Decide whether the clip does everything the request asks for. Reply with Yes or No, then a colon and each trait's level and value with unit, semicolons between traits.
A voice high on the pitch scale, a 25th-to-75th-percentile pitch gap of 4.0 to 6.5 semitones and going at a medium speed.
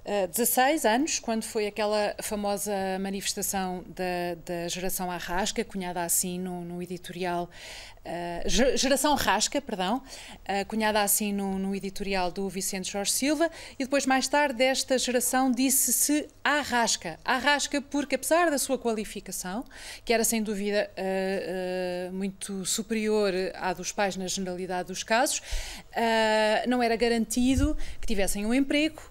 Yes: high, 210 Hz; average, 5.1 semitones; average, 130 wpm